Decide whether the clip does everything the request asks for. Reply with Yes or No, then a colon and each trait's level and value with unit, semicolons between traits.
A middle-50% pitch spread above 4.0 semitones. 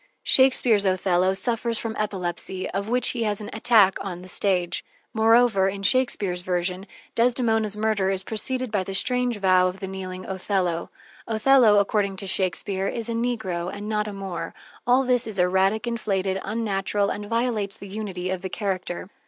No: average, 3.1 semitones